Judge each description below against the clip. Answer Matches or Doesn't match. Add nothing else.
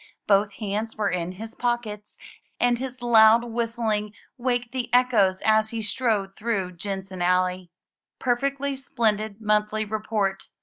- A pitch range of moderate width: Matches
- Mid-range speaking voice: Doesn't match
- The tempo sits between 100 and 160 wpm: Matches